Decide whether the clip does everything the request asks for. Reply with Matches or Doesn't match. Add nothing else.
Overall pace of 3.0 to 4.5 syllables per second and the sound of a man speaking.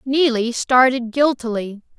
Doesn't match